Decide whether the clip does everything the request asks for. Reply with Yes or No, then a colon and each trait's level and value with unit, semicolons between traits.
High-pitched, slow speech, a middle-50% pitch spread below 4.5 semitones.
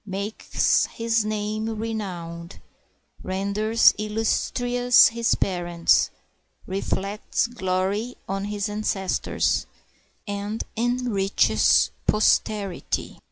Yes: high, 210 Hz; slow, 70 wpm; narrow, 2.5 semitones